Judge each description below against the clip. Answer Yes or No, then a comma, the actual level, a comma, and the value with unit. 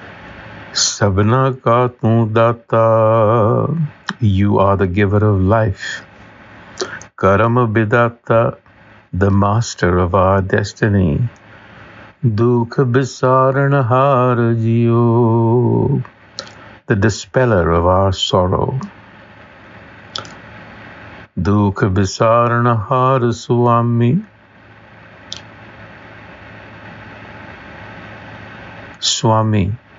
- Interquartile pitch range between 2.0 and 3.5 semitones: Yes, average, 2.9 semitones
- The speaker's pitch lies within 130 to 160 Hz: No, low, 110 Hz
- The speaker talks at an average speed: No, slow, 60 wpm